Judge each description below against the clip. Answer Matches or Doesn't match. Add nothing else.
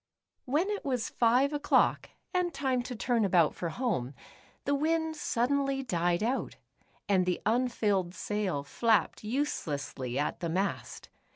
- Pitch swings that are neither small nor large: Doesn't match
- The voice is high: Matches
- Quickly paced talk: Doesn't match